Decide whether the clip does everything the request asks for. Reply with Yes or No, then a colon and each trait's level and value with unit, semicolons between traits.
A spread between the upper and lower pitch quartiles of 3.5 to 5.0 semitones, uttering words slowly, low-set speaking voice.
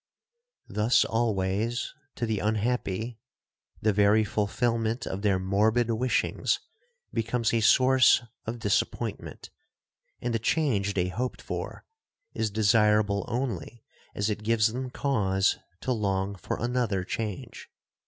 No: average, 2.8 semitones; slow, 120 wpm; low, 110 Hz